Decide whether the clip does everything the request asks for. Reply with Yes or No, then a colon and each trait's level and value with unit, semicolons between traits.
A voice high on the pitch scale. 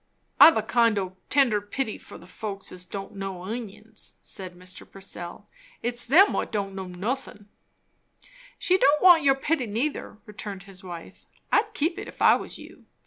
Yes: high, 210 Hz